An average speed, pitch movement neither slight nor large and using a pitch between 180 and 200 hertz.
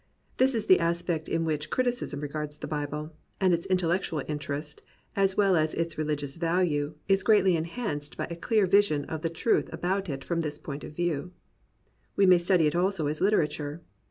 No: average, 185 wpm; average, 3.9 semitones; medium, 165 Hz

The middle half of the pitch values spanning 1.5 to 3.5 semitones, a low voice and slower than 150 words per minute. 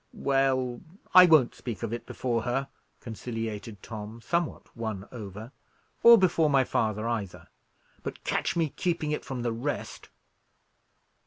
No: average, 4.3 semitones; low, 120 Hz; average, 140 wpm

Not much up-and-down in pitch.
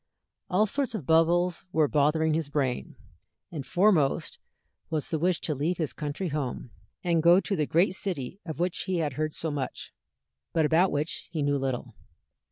No: average, 3.3 semitones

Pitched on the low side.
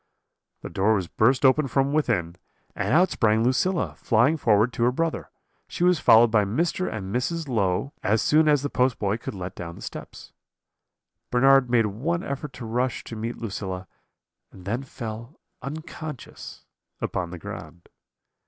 Yes: low, 120 Hz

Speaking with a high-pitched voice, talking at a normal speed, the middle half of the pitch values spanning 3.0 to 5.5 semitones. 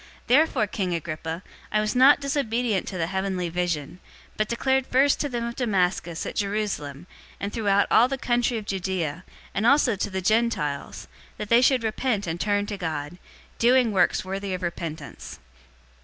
Yes: high, 205 Hz; average, 175 wpm; average, 5.1 semitones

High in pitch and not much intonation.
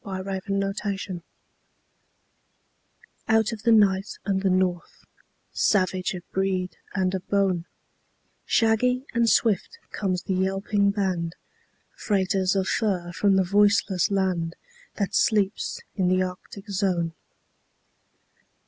Yes: high, 195 Hz; narrow, 1.8 semitones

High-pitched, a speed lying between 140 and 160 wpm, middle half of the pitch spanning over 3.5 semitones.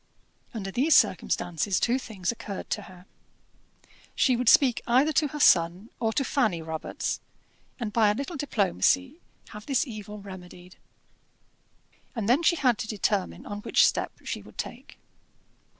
Yes: high, 220 Hz; average, 150 wpm; average, 5.3 semitones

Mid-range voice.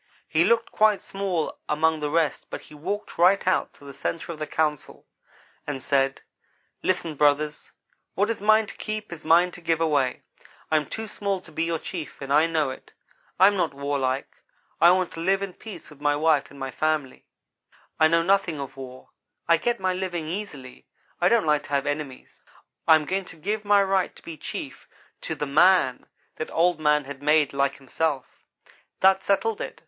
Yes: medium, 160 Hz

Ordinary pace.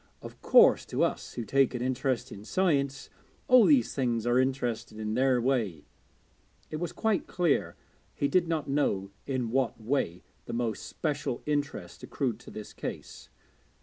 Yes: average, 160 wpm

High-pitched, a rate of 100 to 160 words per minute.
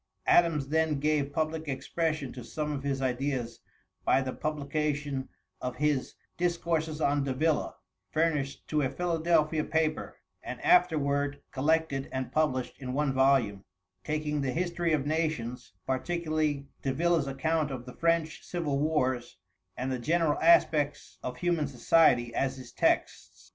No: medium, 150 Hz; average, 140 wpm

